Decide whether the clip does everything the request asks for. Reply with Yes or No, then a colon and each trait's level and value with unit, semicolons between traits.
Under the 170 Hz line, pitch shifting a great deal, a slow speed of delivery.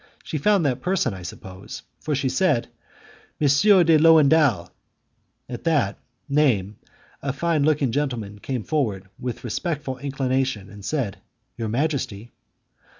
Yes: low, 135 Hz; wide, 5.7 semitones; slow, 130 wpm